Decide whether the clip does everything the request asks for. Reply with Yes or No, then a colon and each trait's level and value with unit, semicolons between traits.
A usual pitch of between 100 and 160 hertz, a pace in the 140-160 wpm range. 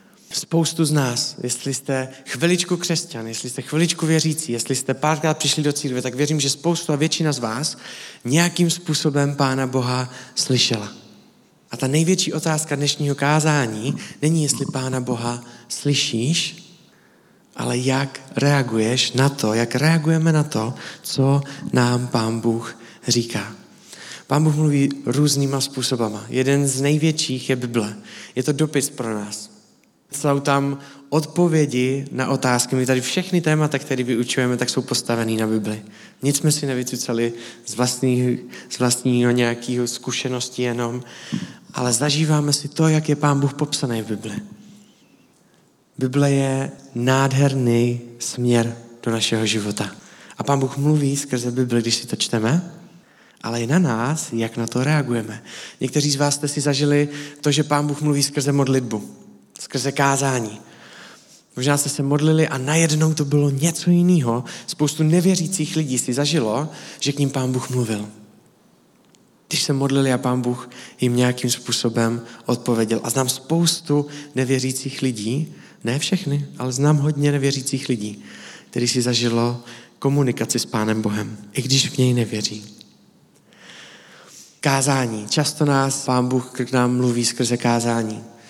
Yes: low, 135 Hz; average, 145 wpm